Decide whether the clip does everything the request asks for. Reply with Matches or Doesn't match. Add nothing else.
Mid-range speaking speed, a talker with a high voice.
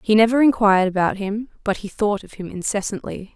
Matches